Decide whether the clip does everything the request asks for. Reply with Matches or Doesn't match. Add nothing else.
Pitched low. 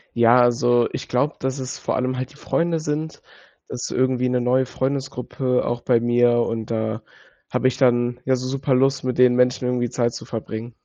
Matches